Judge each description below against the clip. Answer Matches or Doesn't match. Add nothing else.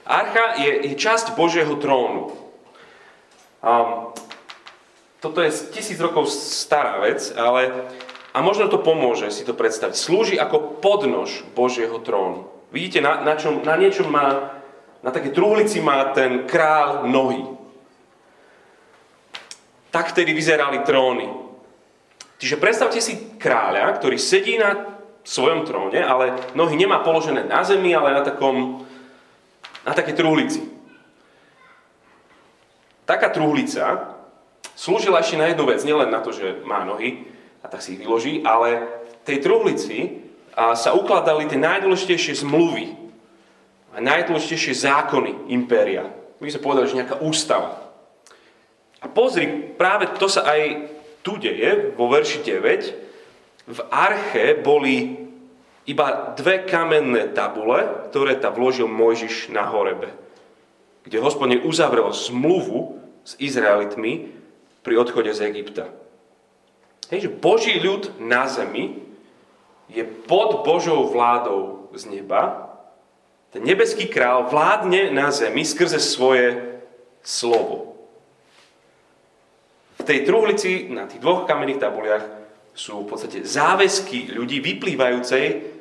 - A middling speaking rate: Matches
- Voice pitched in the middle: Matches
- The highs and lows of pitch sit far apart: Matches